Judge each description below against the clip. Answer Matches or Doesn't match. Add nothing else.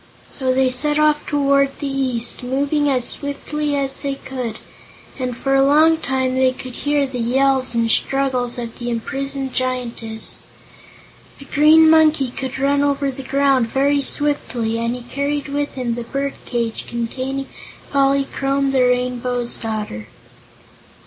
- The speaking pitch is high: Matches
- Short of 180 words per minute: Matches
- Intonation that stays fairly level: Matches